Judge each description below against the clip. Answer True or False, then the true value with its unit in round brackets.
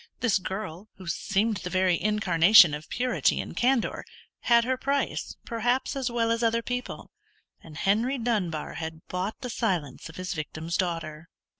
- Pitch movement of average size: False (5.7 semitones)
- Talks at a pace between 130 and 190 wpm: True (160 wpm)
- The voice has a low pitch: False (200 Hz)